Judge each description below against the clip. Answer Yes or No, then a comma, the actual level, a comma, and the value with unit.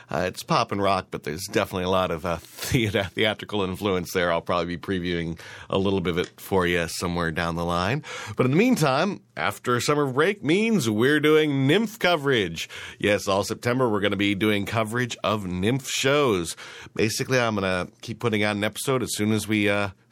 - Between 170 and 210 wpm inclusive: Yes, fast, 205 wpm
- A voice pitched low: Yes, low, 100 Hz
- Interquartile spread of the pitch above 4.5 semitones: Yes, average, 4.9 semitones